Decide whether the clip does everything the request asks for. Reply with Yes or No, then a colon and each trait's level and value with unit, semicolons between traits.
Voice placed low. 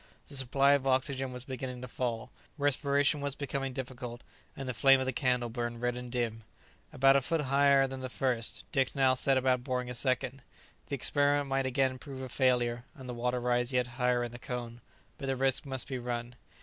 Yes: low, 130 Hz